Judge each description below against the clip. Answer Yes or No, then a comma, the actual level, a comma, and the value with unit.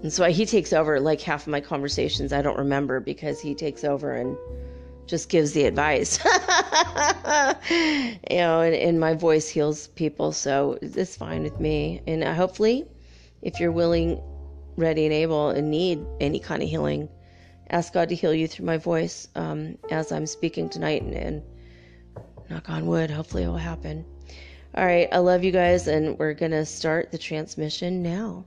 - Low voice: No, medium, 155 Hz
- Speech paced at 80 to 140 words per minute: No, average, 180 wpm